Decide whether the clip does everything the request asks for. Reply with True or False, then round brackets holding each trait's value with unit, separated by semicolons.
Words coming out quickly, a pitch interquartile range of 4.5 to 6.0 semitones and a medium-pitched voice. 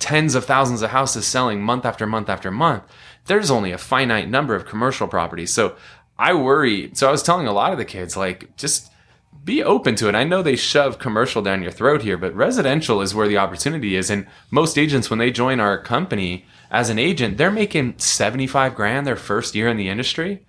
False (215 wpm; 4.9 semitones; 115 Hz)